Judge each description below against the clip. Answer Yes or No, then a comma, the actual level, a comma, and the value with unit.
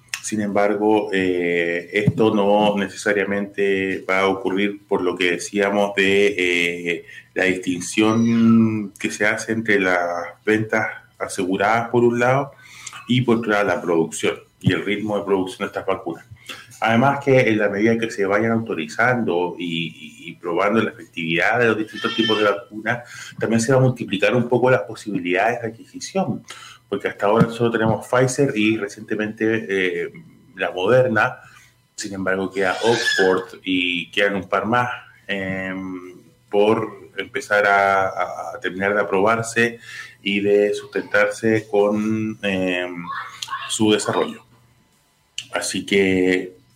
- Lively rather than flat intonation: No, average, 2.9 semitones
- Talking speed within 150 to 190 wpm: No, average, 140 wpm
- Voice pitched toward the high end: No, low, 105 Hz